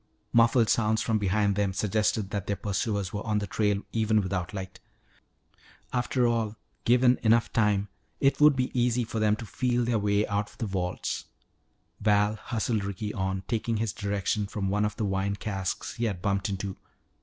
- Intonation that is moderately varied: No, narrow, 2.3 semitones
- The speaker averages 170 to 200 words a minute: Yes, average, 180 wpm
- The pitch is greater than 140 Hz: No, low, 105 Hz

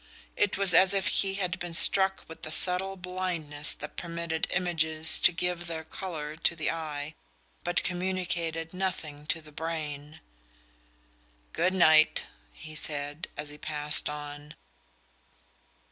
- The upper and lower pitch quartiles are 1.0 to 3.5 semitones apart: Yes, average, 3.1 semitones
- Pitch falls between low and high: Yes, medium, 165 Hz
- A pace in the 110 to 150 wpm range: Yes, slow, 135 wpm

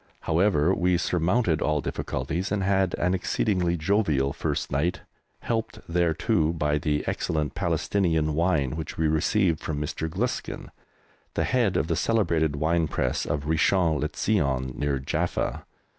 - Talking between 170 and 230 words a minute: No, average, 145 wpm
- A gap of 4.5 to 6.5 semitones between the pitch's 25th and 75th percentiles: No, average, 3.8 semitones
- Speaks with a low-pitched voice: Yes, very low, 80 Hz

